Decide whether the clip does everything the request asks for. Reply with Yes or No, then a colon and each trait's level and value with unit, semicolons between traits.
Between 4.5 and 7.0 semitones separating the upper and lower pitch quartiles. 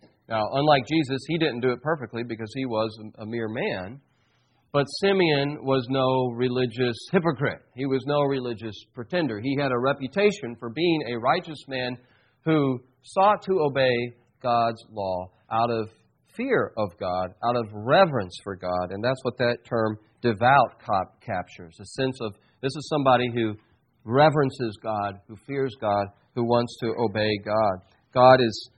No: average, 3.4 semitones